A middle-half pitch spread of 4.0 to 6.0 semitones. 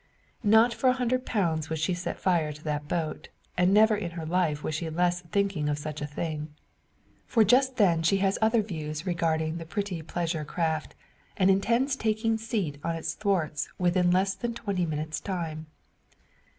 Yes: average, 4.6 semitones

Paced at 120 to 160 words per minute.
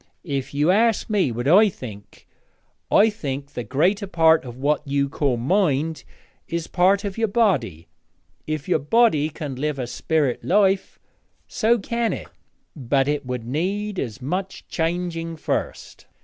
Yes: average, 150 wpm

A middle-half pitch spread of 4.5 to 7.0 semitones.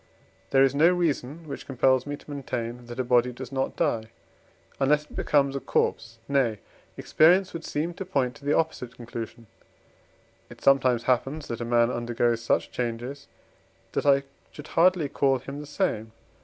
No: average, 3.6 semitones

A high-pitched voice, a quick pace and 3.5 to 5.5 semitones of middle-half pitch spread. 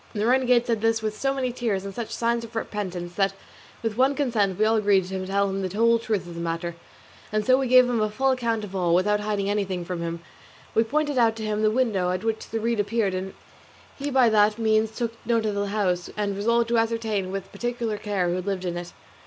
No: high, 215 Hz; fast, 240 wpm; average, 3.1 semitones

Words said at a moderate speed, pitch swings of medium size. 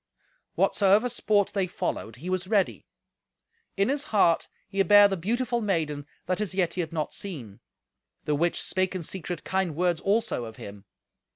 Yes: average, 170 wpm; average, 3.9 semitones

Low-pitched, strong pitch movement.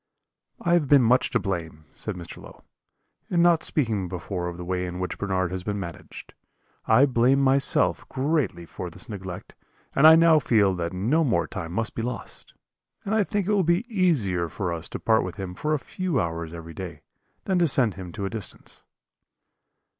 Yes: low, 110 Hz; wide, 8.8 semitones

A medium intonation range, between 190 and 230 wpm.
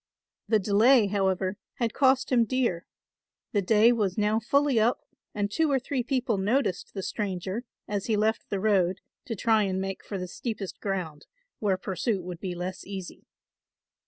No: average, 3.6 semitones; average, 170 wpm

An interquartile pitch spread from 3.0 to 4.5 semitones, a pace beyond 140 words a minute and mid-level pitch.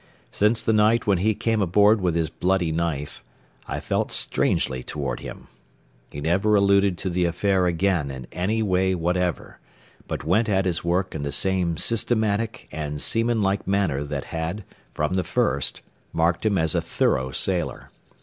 No: average, 3.8 semitones; average, 170 wpm; very low, 90 Hz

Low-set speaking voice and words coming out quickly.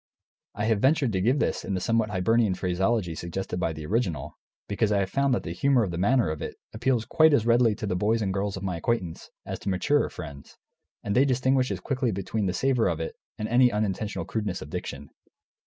Yes: low, 105 Hz; fast, 225 wpm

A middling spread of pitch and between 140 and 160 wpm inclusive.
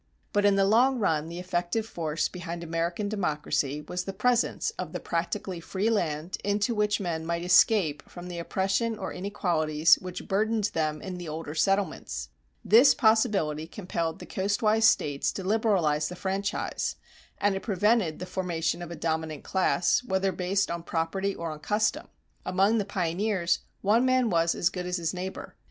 No: average, 3.7 semitones; average, 170 wpm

